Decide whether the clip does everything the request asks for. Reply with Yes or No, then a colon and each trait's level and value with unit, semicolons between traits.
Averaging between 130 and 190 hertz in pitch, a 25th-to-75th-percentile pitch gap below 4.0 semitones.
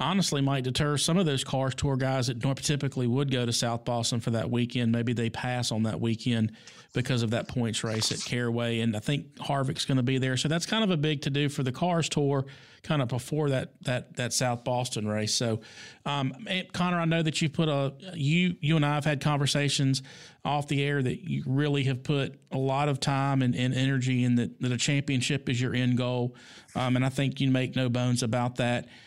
Yes: low, 135 Hz; average, 2.8 semitones